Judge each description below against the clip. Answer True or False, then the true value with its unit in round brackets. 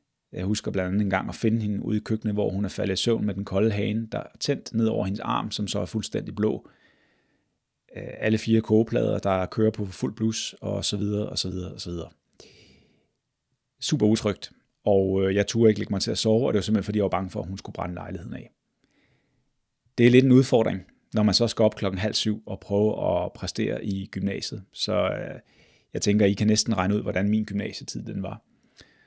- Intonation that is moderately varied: False (2.2 semitones)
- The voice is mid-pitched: False (105 Hz)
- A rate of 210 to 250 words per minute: True (225 wpm)